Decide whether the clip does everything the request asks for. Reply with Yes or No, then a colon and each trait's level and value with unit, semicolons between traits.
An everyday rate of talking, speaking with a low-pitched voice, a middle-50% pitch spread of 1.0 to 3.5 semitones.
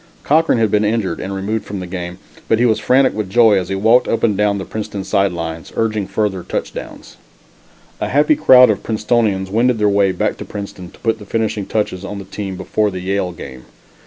No: fast, 220 wpm; low, 105 Hz; average, 2.8 semitones